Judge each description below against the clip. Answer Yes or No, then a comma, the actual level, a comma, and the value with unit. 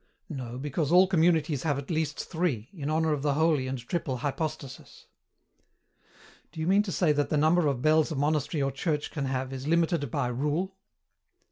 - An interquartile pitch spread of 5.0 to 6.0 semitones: No, average, 3.1 semitones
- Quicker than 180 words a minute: Yes, average, 190 wpm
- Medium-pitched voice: Yes, medium, 150 Hz